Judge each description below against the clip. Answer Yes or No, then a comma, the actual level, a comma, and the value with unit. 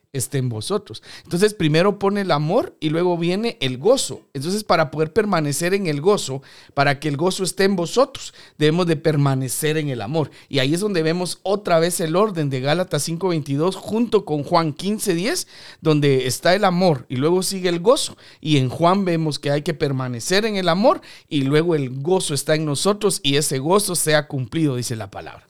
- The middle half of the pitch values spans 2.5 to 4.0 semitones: No, average, 4.5 semitones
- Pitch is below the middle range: No, medium, 160 Hz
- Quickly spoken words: Yes, fast, 200 wpm